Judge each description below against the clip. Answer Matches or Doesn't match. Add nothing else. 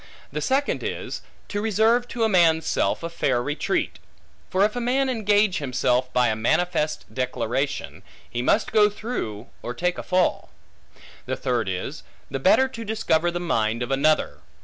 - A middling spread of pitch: Doesn't match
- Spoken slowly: Doesn't match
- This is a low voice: Doesn't match